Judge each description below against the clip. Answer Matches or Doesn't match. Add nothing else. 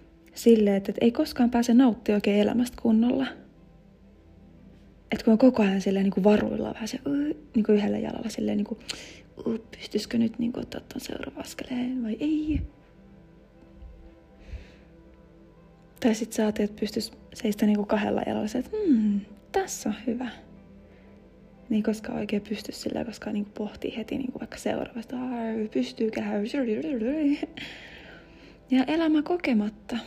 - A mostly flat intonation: Doesn't match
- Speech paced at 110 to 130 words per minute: Doesn't match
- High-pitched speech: Matches